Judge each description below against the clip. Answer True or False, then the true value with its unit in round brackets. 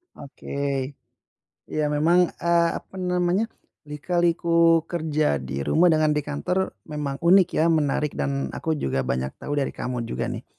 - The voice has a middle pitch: True (155 Hz)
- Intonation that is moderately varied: True (3.6 semitones)